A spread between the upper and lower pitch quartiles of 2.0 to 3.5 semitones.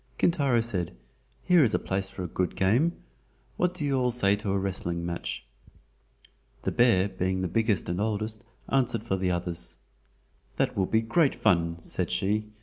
No: average, 4.7 semitones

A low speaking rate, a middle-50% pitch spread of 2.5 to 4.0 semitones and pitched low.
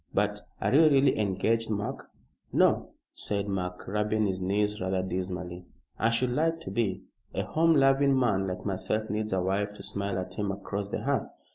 No: average, 180 wpm; average, 3.4 semitones; low, 105 Hz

